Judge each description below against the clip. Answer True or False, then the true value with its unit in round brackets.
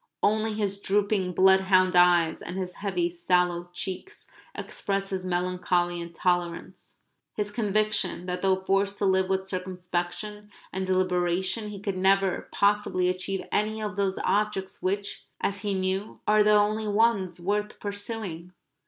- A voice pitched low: False (190 Hz)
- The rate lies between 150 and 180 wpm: False (140 wpm)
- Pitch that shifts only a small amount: True (2.3 semitones)